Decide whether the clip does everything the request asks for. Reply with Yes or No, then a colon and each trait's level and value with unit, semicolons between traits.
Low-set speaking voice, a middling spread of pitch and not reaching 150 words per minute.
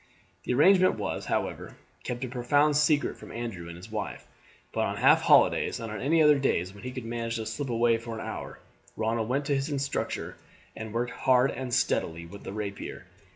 No: low, 120 Hz; average, 3.8 semitones; average, 200 wpm